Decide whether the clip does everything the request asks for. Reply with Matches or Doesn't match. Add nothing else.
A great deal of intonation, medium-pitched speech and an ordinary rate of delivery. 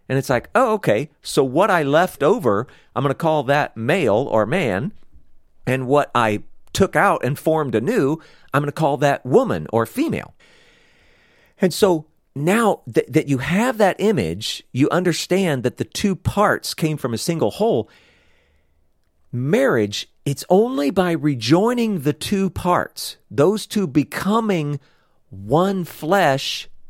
Matches